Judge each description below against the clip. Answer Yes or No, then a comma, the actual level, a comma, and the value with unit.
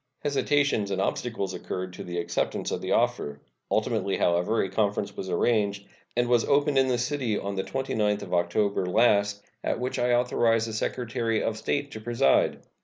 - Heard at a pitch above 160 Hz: No, low, 110 Hz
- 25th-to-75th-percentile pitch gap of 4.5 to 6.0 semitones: No, average, 3.8 semitones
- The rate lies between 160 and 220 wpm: Yes, average, 180 wpm